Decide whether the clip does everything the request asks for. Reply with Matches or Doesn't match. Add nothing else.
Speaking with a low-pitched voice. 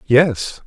Matches